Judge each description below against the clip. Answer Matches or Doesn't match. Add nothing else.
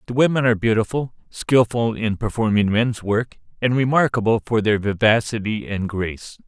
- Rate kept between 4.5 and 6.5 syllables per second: Matches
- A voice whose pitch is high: Doesn't match